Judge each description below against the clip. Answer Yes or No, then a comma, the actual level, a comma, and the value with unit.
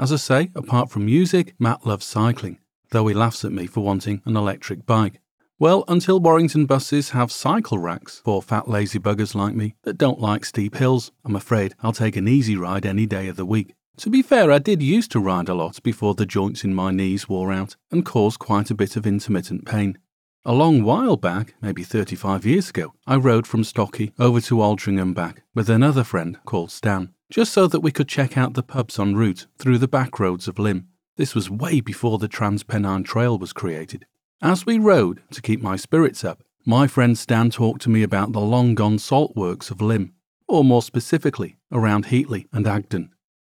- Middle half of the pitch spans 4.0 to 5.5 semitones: Yes, average, 4.4 semitones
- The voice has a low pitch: Yes, low, 110 Hz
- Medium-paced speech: No, fast, 210 wpm